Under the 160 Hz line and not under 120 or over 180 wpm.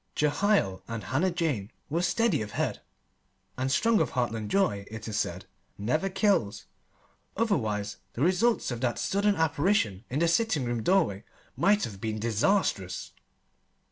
Yes: low, 135 Hz; average, 145 wpm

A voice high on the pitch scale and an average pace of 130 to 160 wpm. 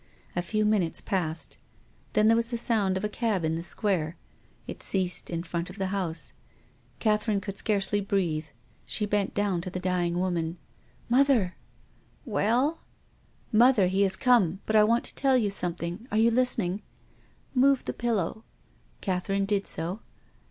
No: high, 200 Hz; average, 185 wpm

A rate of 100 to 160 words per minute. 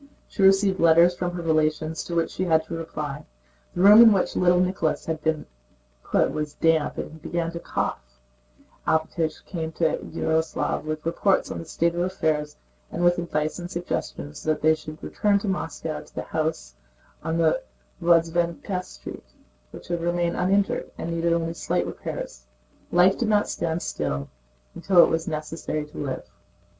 No: average, 175 wpm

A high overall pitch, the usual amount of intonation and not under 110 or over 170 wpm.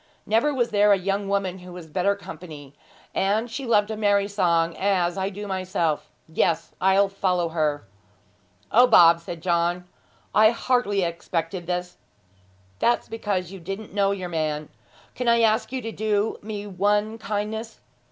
Yes: high, 195 Hz; average, 3.3 semitones; average, 160 wpm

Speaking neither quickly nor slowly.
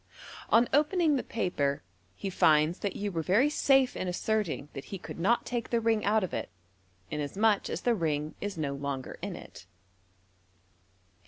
Yes: average, 170 wpm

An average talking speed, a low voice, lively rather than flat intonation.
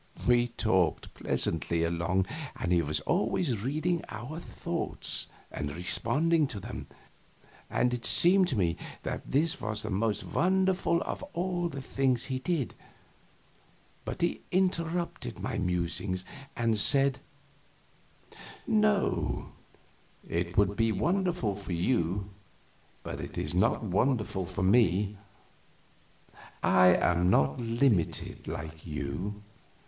No: slow, 120 wpm; low, 110 Hz; wide, 8.9 semitones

